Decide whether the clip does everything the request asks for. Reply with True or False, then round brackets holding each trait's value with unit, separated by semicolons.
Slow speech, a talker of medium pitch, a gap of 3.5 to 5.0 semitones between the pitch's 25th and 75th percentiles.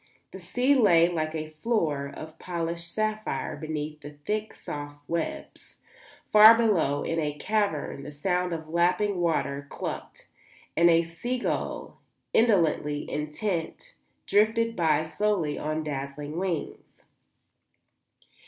False (120 wpm; 165 Hz; 5.5 semitones)